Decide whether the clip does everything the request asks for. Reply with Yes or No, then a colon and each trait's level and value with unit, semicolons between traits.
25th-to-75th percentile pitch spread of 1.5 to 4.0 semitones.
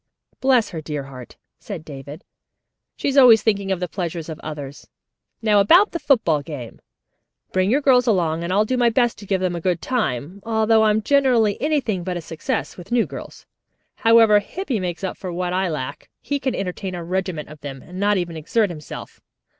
No: wide, 5.5 semitones